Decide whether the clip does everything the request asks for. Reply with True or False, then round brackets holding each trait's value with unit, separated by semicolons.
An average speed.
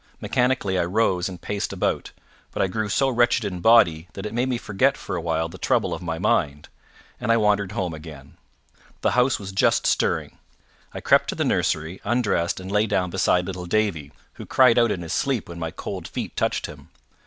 False (210 wpm)